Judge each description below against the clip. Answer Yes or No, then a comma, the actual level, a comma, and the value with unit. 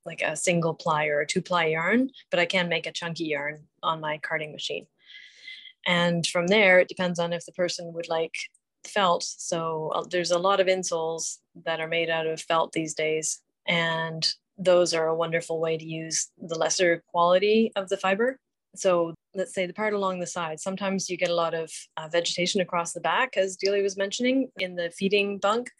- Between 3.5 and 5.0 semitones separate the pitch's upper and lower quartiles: No, average, 2.8 semitones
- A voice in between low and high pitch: Yes, medium, 175 Hz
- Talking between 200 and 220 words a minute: Yes, fast, 205 wpm